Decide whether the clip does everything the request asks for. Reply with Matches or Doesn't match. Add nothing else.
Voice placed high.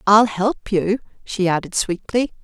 Matches